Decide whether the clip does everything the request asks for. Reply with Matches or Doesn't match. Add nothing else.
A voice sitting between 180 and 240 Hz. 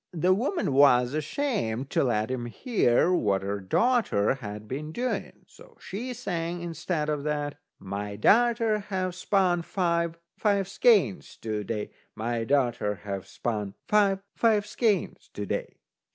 Doesn't match